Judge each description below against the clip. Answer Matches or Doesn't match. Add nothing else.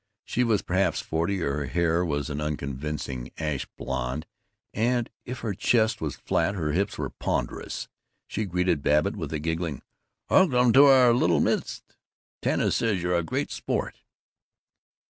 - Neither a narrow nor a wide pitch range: Doesn't match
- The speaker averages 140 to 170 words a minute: Matches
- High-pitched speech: Doesn't match